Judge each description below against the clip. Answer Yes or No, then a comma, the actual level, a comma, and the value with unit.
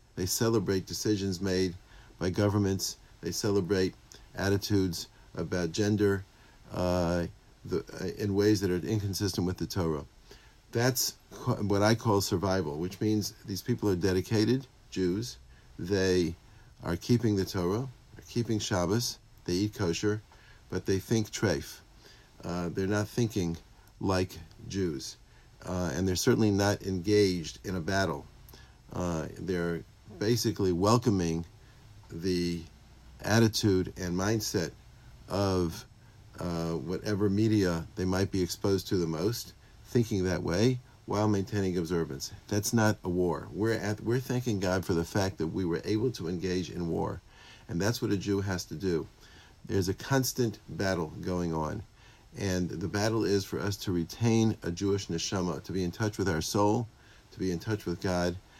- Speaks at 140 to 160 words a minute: Yes, average, 150 wpm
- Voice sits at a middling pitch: No, low, 100 Hz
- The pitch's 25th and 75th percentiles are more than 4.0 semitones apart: No, average, 3.4 semitones